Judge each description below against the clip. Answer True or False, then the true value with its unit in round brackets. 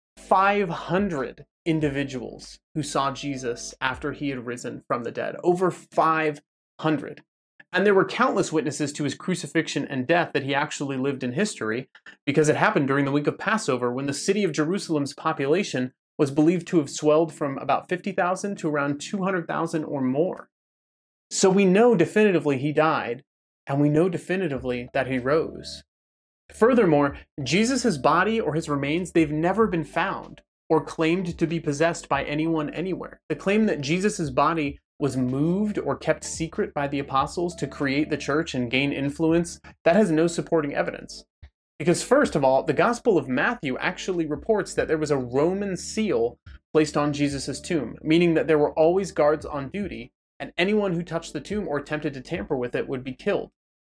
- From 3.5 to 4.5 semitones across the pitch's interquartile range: True (4.0 semitones)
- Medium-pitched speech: True (155 Hz)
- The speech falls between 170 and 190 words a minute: True (175 wpm)